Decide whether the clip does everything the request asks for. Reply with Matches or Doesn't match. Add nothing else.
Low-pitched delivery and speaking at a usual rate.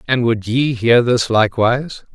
Matches